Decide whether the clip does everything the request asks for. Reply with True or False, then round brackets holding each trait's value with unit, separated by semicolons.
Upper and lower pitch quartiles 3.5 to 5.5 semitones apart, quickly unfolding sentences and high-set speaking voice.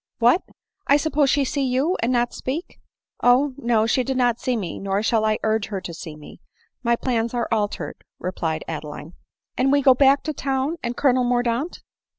True (3.8 semitones; 210 wpm; 245 Hz)